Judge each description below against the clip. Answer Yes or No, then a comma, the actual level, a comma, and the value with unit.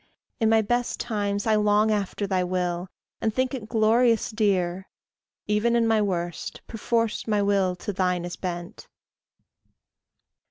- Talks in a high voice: Yes, high, 210 Hz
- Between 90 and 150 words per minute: Yes, average, 145 wpm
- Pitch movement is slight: No, average, 3.3 semitones